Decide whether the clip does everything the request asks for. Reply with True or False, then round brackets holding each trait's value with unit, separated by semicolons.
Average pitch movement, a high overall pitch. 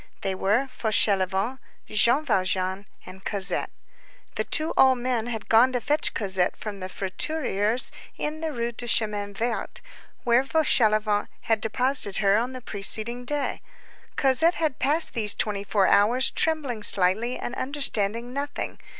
True (4.3 semitones; 230 Hz)